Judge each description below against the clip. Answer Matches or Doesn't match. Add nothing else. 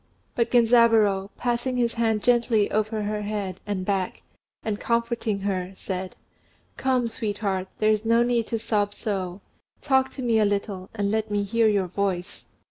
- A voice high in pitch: Matches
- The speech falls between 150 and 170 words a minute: Matches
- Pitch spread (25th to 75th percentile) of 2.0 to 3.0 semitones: Matches